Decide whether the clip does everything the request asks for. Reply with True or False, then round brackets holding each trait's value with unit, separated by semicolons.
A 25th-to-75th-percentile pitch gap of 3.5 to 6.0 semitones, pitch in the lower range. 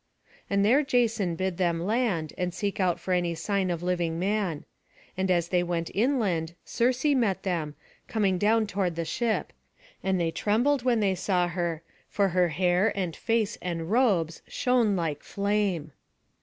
False (3.9 semitones; 190 Hz)